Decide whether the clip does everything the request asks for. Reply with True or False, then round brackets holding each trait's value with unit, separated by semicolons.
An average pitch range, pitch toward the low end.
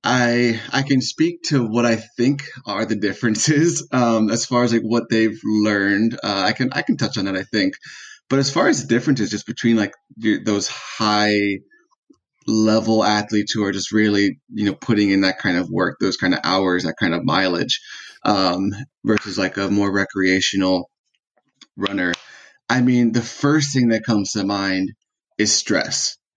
True (3.4 semitones; 110 Hz)